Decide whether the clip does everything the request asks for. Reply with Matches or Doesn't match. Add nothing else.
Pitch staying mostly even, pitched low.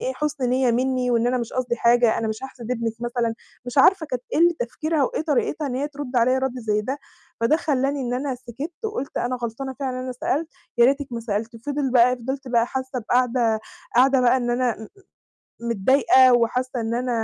Doesn't match